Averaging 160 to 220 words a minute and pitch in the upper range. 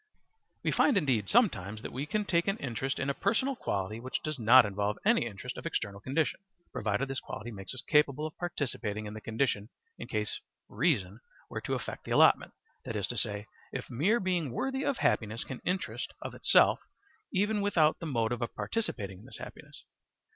No: average, 190 wpm; low, 130 Hz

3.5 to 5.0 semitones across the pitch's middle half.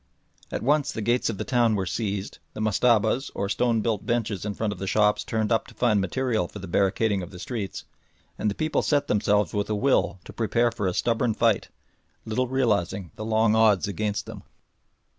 No: average, 2.7 semitones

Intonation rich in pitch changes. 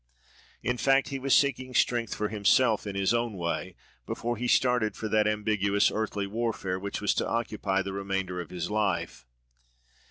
No: average, 3.3 semitones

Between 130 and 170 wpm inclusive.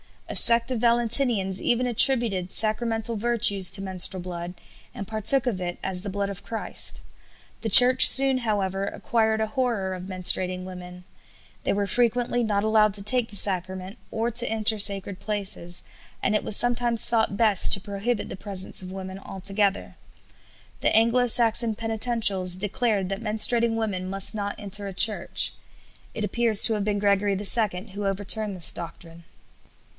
Yes: average, 160 wpm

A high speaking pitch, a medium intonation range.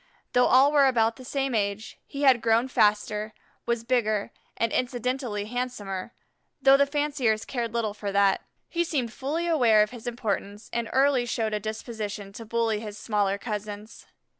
Yes: high, 230 Hz; average, 3.3 semitones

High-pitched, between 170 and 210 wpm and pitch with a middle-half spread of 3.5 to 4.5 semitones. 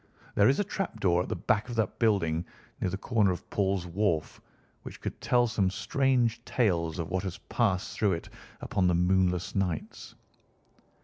No: very low, 95 Hz; average, 180 wpm; average, 4.0 semitones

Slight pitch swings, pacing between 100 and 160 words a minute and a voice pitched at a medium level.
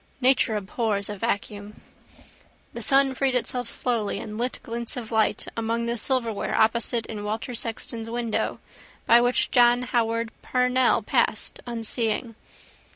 No: narrow, 1.8 semitones; slow, 135 wpm; high, 235 Hz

